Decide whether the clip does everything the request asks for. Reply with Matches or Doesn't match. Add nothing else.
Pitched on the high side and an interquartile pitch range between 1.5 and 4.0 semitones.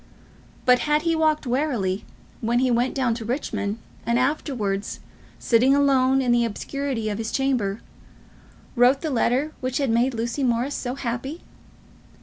Matches